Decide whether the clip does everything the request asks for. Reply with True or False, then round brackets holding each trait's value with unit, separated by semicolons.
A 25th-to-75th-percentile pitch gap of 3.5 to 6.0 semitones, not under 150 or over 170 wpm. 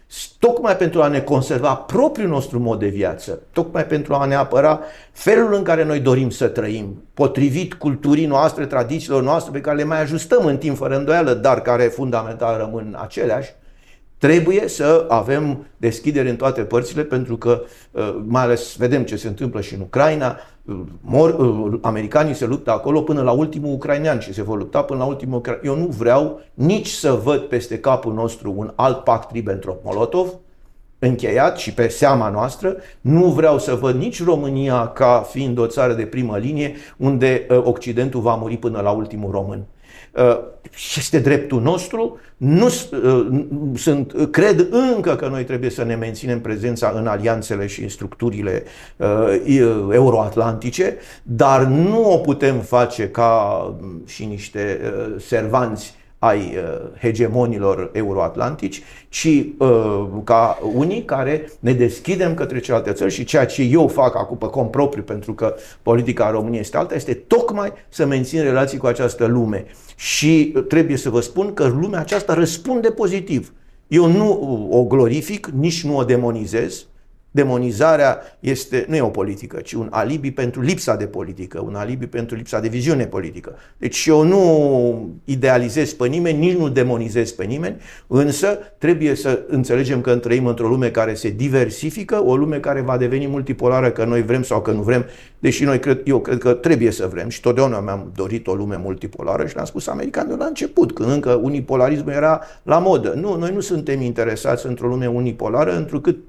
True (4.5 semitones; 165 wpm)